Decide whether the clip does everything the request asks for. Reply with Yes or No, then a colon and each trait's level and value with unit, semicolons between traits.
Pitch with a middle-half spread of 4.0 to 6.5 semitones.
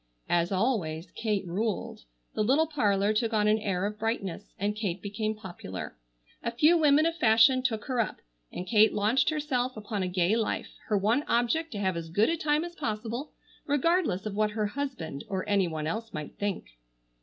Yes: average, 4.7 semitones